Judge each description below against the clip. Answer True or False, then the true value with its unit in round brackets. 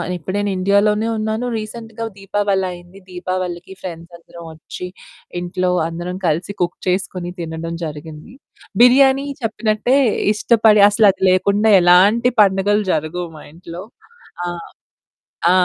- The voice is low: False (185 Hz)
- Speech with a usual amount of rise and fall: True (3.4 semitones)